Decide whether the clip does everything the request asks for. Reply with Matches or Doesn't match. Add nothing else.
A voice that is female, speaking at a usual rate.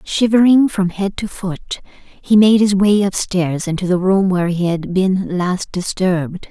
Matches